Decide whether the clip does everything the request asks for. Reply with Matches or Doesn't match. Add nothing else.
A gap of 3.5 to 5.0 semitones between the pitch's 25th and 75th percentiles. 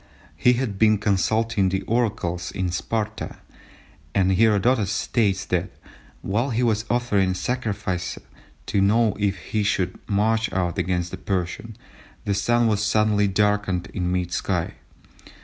Doesn't match